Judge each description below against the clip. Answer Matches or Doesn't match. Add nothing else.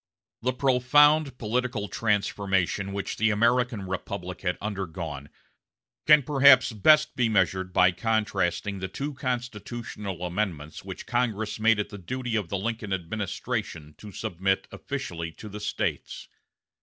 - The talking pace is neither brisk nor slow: Doesn't match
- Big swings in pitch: Doesn't match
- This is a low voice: Matches